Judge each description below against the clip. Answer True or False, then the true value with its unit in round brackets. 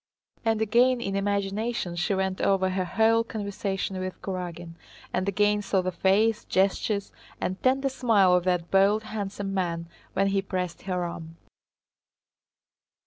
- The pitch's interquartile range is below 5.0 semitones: True (2.5 semitones)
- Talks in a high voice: True (195 Hz)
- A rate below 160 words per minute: True (140 wpm)